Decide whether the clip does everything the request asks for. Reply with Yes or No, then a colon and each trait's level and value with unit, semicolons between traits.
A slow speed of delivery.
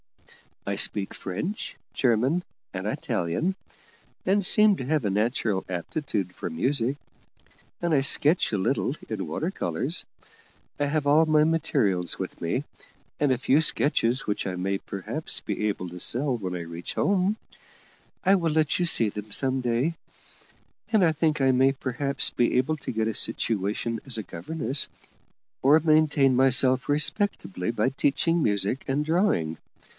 No: average, 155 wpm